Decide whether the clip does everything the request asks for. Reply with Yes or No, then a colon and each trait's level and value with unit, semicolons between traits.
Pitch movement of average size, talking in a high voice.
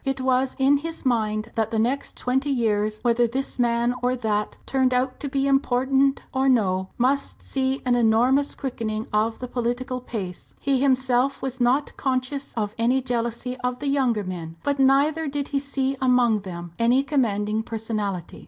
Yes: average, 3.2 semitones; very high, 250 Hz